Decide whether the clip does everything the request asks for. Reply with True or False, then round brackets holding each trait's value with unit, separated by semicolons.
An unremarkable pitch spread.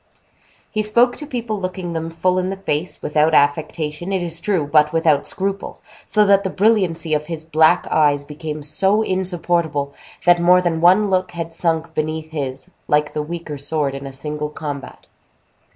True (3.7 semitones)